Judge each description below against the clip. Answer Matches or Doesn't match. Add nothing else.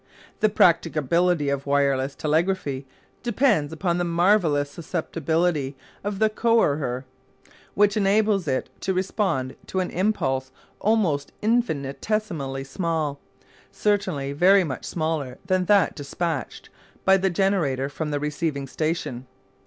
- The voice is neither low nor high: Matches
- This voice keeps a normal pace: Doesn't match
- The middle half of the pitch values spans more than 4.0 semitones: Matches